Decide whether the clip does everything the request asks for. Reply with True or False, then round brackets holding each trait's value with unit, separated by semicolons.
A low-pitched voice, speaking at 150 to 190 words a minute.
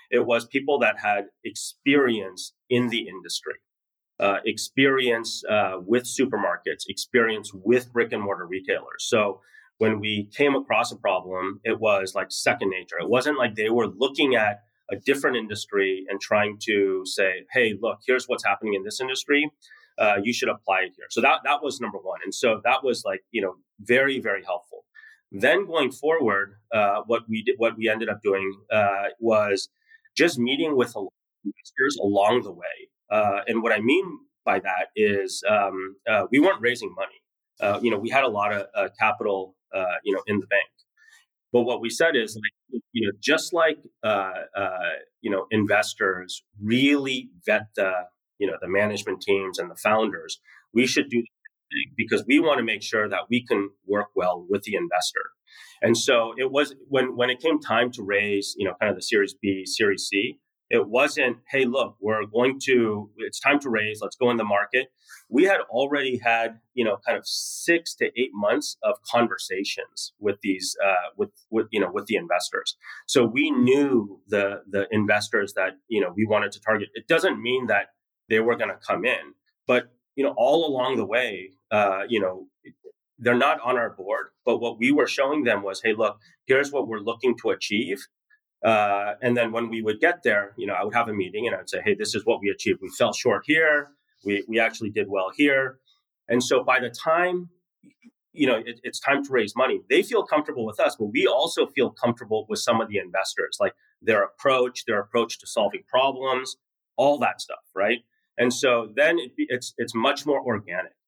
False (120 Hz; 200 wpm)